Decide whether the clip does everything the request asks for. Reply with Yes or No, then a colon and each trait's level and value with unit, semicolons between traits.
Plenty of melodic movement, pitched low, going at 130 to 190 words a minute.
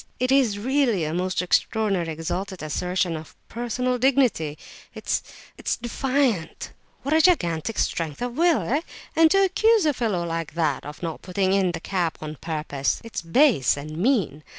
No: wide, 7.8 semitones; high, 190 Hz; average, 160 wpm